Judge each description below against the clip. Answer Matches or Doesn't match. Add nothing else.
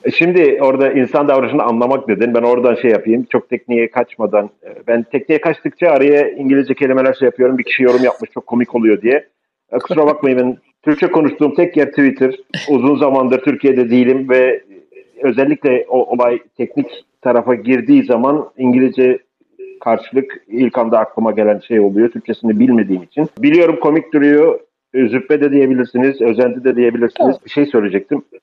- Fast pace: Matches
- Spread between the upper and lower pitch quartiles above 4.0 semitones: Doesn't match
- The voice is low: Matches